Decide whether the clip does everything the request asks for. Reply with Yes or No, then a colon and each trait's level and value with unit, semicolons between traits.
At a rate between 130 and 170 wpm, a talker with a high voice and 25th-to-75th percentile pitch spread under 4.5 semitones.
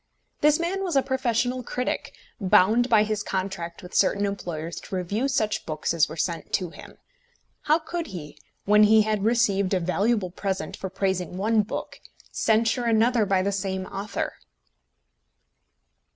Yes: average, 155 wpm; high, 205 Hz; average, 3.9 semitones